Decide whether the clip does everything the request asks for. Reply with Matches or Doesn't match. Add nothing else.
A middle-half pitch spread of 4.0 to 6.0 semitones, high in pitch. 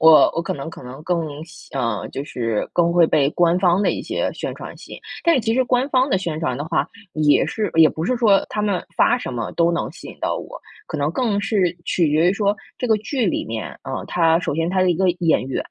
Doesn't match